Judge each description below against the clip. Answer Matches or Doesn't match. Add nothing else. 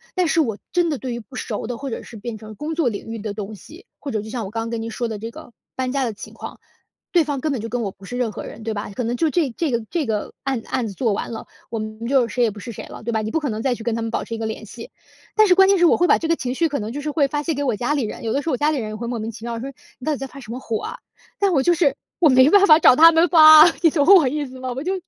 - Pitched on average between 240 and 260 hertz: Matches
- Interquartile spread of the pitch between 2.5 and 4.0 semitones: Doesn't match